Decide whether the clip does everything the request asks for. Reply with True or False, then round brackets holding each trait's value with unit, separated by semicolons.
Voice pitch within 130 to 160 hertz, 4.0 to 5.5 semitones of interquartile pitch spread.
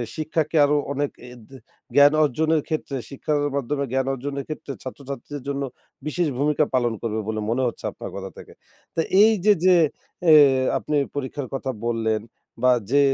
False (140 Hz; 2.8 semitones)